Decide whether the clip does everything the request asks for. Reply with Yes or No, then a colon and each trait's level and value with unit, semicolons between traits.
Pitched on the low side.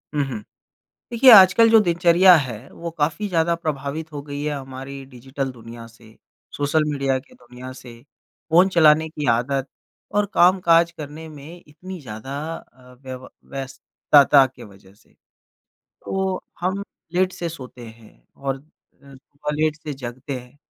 No: medium, 145 Hz